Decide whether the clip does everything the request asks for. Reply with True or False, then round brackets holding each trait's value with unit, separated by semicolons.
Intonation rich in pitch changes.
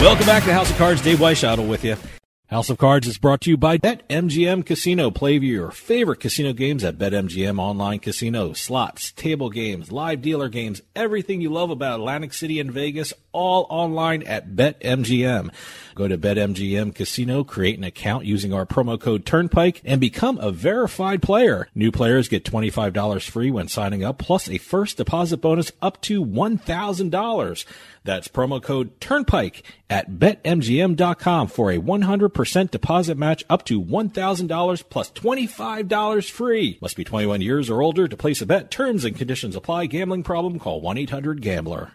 True (8.1 semitones)